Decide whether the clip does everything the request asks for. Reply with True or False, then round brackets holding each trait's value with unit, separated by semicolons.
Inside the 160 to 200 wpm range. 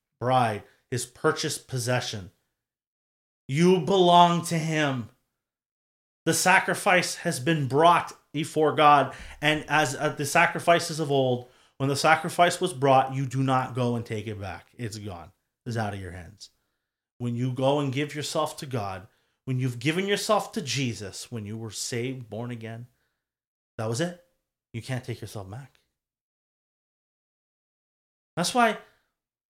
False (150 wpm)